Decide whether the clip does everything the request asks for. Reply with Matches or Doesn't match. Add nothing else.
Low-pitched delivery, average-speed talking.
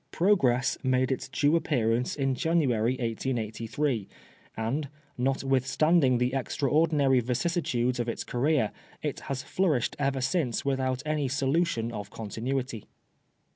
Doesn't match